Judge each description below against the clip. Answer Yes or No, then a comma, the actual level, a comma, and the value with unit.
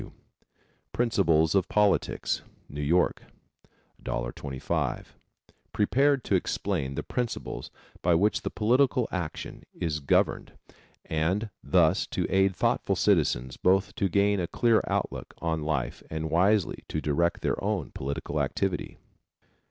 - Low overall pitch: Yes, very low, 90 Hz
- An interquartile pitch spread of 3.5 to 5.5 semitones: Yes, average, 4.8 semitones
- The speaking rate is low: Yes, slow, 120 wpm